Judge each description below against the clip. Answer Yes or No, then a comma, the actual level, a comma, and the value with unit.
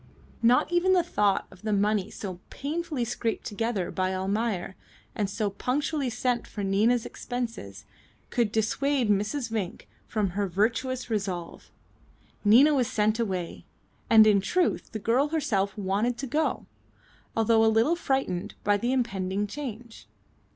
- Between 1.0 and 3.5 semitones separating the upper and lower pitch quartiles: No, average, 4.0 semitones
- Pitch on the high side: Yes, high, 220 Hz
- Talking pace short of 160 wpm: Yes, average, 145 wpm